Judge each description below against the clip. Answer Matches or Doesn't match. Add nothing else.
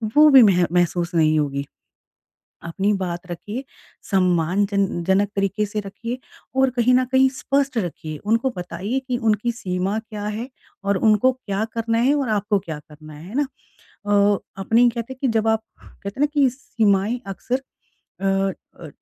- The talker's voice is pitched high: Matches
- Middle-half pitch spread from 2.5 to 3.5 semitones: Doesn't match